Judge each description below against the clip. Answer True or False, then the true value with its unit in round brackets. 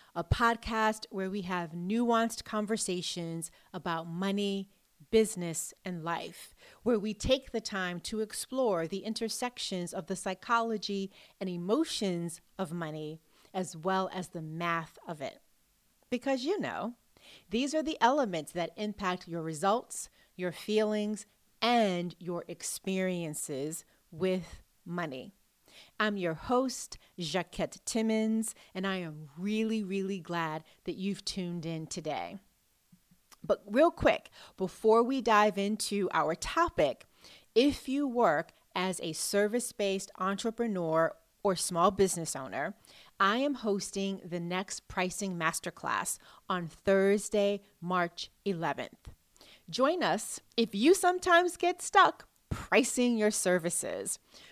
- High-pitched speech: True (195 Hz)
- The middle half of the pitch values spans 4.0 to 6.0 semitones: True (4.3 semitones)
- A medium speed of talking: False (120 wpm)